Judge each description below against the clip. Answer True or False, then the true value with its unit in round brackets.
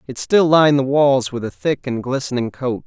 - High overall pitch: False (135 Hz)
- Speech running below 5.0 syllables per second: False (5.2 syllables/s)